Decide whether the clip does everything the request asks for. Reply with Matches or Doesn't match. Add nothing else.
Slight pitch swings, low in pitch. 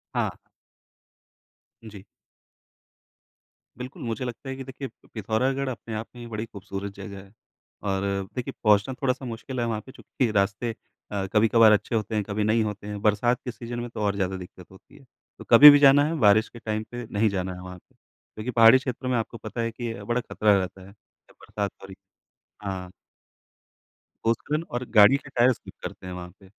Doesn't match